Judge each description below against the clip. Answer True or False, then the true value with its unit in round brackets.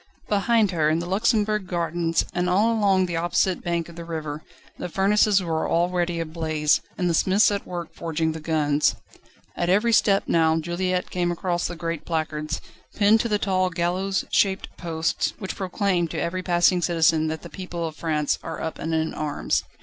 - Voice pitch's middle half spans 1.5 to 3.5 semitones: True (2.8 semitones)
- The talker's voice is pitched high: False (175 Hz)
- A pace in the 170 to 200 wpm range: True (185 wpm)